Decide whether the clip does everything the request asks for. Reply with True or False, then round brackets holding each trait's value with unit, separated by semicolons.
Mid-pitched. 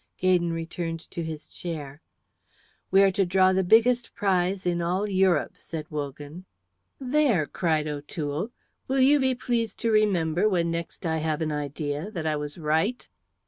True (175 Hz)